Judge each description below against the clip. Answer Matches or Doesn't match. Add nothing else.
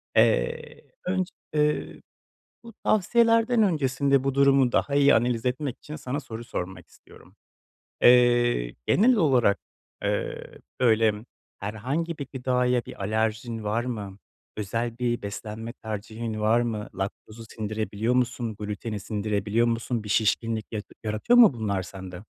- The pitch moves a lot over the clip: Doesn't match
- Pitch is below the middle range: Matches